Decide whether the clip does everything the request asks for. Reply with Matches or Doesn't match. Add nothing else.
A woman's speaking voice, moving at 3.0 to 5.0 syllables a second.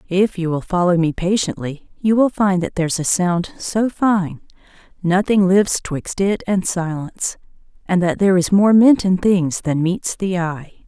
Matches